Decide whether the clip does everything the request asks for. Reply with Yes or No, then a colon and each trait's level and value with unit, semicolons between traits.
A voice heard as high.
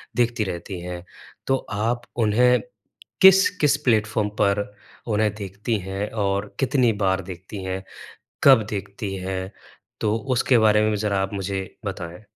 No: low, 105 Hz